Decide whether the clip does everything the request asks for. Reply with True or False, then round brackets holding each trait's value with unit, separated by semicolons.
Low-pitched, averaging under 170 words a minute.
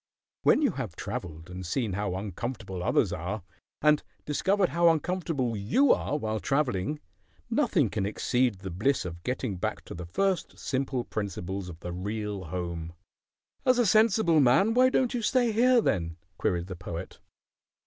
True (110 Hz; 160 wpm)